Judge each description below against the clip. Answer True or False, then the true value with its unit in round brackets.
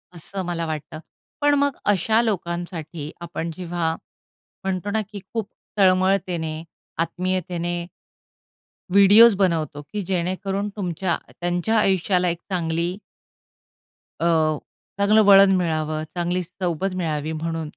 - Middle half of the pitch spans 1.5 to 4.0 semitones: True (2.8 semitones)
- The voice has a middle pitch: True (175 Hz)